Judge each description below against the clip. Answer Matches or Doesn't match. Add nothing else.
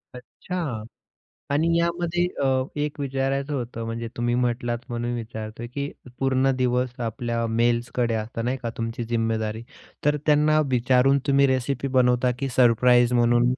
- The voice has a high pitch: Doesn't match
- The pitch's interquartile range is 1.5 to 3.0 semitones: Matches